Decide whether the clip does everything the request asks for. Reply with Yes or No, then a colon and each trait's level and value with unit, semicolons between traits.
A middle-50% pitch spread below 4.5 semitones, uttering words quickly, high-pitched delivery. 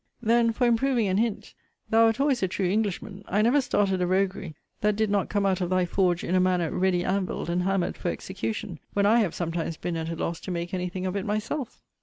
Yes: average, 3.3 semitones; fast, 240 wpm; high, 195 Hz